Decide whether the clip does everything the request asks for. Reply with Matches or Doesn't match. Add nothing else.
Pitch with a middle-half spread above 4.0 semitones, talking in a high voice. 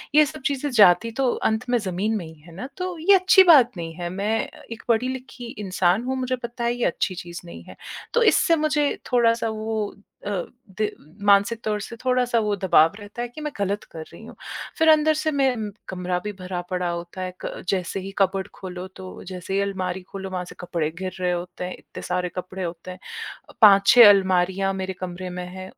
Matches